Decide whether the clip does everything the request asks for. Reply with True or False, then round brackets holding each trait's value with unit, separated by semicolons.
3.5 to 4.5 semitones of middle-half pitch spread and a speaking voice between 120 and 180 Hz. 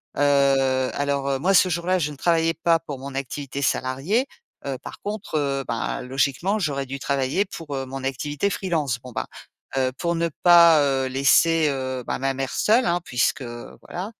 True (3.9 semitones; 140 Hz)